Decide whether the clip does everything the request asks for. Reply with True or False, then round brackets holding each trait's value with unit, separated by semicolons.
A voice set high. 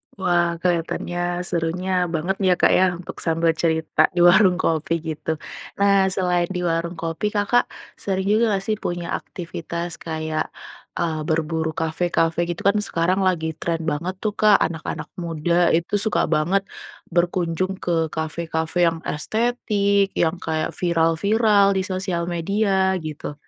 False (175 Hz)